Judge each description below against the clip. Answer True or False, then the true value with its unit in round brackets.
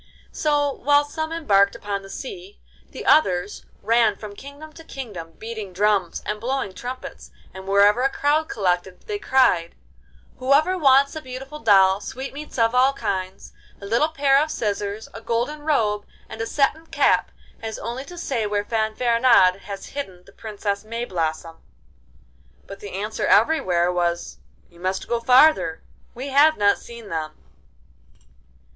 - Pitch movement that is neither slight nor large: False (5.9 semitones)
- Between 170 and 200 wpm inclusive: False (150 wpm)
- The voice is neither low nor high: False (225 Hz)